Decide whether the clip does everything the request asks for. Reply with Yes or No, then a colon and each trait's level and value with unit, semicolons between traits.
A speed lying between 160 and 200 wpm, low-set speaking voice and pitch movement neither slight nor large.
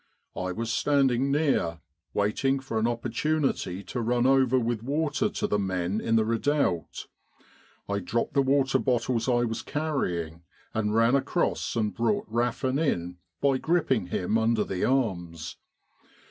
No: average, 145 wpm; low, 120 Hz; average, 4.6 semitones